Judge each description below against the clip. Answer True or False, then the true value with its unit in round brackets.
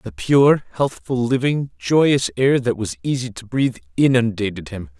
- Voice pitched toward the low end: True (125 Hz)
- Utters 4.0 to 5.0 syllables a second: True (4.6 syllables/s)